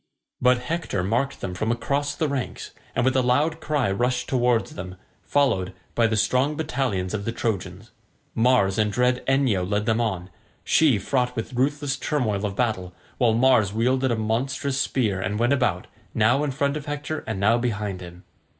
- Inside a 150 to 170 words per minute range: No, average, 180 wpm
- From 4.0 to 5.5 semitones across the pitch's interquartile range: Yes, average, 4.4 semitones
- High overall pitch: No, low, 120 Hz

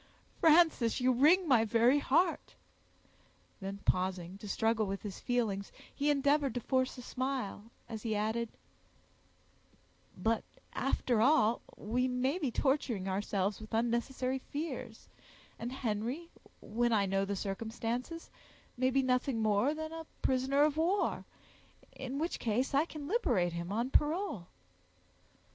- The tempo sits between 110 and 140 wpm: Yes, slow, 135 wpm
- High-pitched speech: Yes, high, 245 Hz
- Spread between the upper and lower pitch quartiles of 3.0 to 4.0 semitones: No, average, 4.7 semitones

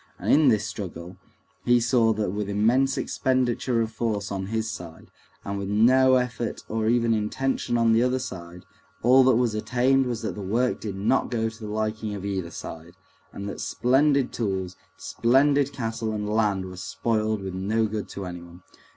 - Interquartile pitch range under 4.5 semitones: Yes, average, 3.6 semitones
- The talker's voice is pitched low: Yes, low, 110 Hz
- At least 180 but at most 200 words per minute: Yes, average, 185 wpm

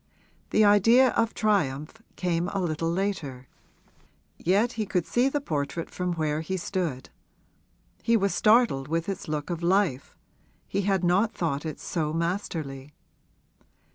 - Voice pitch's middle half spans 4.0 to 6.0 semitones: Yes, average, 4.7 semitones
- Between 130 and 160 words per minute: Yes, average, 145 wpm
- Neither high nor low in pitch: Yes, medium, 175 Hz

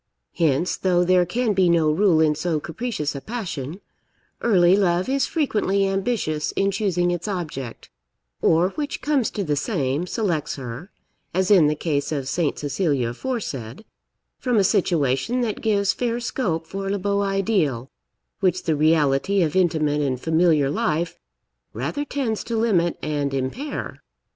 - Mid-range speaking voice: Yes, medium, 175 Hz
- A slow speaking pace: No, average, 155 wpm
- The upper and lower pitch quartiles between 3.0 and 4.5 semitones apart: No, average, 5.1 semitones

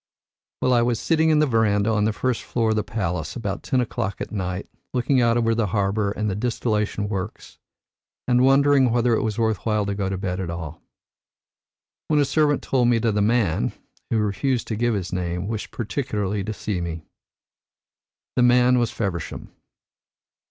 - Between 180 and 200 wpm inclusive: Yes, average, 185 wpm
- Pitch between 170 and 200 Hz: No, low, 110 Hz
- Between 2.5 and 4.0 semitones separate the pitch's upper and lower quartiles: Yes, average, 3.5 semitones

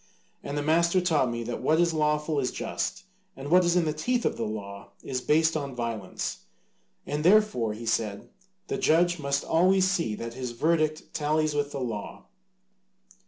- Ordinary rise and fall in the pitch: No, wide, 5.8 semitones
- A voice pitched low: No, medium, 150 Hz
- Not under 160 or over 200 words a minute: Yes, average, 175 wpm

